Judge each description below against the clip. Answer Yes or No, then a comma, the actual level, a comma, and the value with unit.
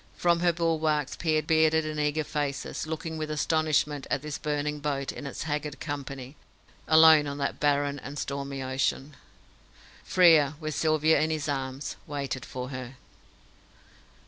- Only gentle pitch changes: Yes, narrow, 2.0 semitones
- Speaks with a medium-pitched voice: Yes, medium, 150 Hz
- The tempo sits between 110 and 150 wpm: Yes, average, 145 wpm